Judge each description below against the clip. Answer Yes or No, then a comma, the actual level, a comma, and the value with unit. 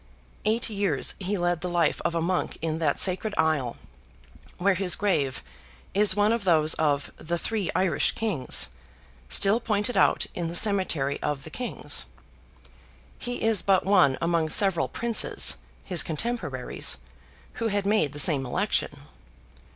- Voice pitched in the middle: Yes, medium, 180 Hz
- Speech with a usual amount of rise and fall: Yes, average, 4.5 semitones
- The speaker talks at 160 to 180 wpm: No, average, 150 wpm